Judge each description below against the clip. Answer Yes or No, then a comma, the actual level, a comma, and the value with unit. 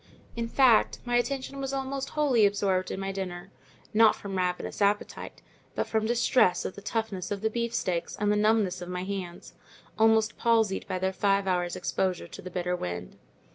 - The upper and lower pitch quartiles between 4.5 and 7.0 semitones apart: No, average, 3.7 semitones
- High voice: Yes, high, 200 Hz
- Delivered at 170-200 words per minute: Yes, average, 180 wpm